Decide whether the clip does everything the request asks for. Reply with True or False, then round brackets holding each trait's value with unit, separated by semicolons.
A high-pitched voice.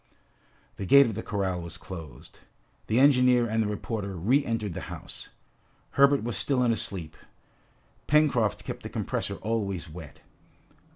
False (110 Hz)